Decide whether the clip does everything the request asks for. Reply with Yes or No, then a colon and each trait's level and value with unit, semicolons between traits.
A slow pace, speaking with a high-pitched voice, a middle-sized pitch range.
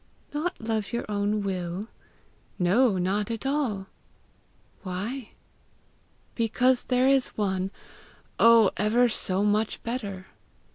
Yes: slow, 105 wpm; high, 215 Hz; average, 4.0 semitones